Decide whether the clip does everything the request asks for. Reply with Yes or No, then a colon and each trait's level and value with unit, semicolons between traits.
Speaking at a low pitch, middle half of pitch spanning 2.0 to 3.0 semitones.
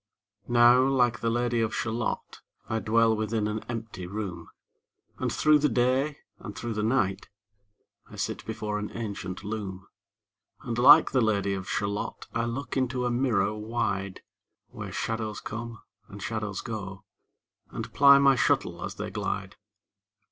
Yes: low, 115 Hz; narrow, 2.6 semitones